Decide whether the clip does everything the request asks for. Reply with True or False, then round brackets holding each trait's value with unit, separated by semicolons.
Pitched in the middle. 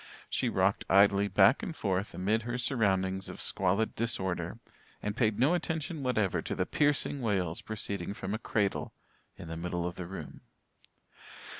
False (100 Hz)